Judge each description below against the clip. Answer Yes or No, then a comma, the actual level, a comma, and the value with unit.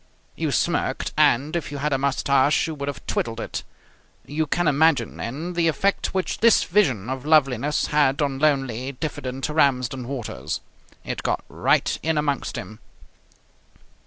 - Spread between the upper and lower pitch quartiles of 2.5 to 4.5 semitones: Yes, average, 3.1 semitones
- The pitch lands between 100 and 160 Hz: Yes, medium, 140 Hz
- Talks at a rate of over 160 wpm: No, average, 155 wpm